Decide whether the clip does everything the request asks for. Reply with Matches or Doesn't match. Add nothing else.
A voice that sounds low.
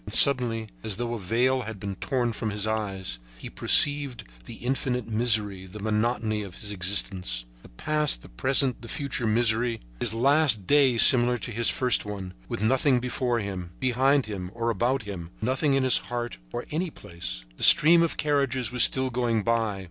Matches